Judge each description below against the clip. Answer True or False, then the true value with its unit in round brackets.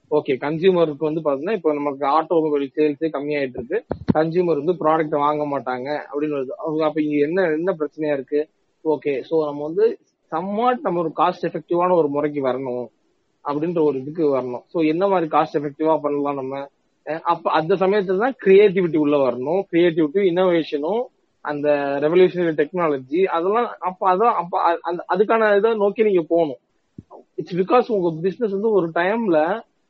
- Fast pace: True (145 wpm)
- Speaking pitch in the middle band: True (160 Hz)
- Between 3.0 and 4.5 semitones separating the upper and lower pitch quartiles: True (4.2 semitones)